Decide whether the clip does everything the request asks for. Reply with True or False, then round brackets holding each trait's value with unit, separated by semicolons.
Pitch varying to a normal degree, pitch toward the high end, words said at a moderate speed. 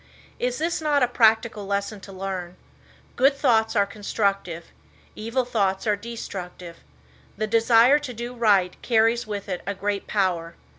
True (3.3 semitones; 215 Hz; 150 wpm)